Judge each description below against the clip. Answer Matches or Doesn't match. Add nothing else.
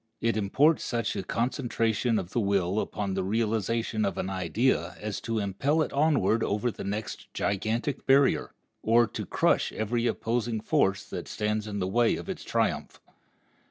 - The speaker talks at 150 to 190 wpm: Matches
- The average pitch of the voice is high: Doesn't match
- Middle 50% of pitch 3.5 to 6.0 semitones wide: Doesn't match